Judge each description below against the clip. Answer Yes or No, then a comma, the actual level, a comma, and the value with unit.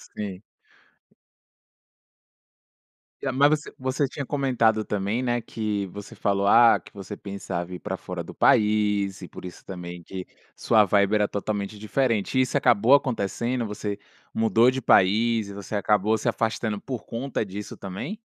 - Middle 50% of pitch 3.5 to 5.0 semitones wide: No, average, 3.0 semitones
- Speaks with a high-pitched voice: No, low, 105 Hz